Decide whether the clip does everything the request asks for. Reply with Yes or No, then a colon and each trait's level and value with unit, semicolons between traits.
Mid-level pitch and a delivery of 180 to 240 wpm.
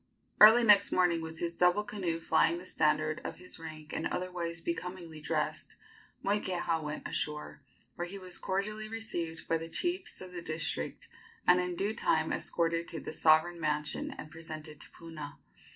No: medium, 170 Hz; average, 170 wpm